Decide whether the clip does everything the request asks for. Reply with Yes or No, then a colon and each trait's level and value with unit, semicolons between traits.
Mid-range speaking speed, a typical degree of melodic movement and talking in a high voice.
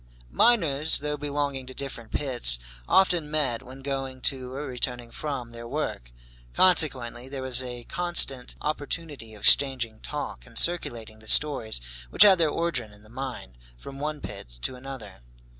No: average, 160 wpm; average, 3.9 semitones; low, 135 Hz